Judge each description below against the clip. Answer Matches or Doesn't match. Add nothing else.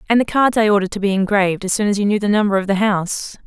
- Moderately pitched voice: Doesn't match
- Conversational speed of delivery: Doesn't match